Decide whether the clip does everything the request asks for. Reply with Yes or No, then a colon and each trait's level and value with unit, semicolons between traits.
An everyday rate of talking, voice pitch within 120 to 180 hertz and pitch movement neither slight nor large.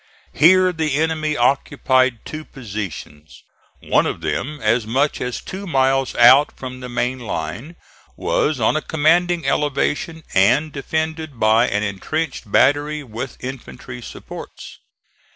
No: slow, 130 wpm; low, 135 Hz; average, 4.4 semitones